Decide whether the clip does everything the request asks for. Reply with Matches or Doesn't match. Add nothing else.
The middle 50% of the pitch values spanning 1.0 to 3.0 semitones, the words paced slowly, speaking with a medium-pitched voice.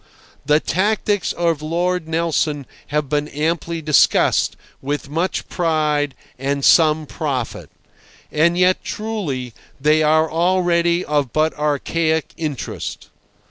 Matches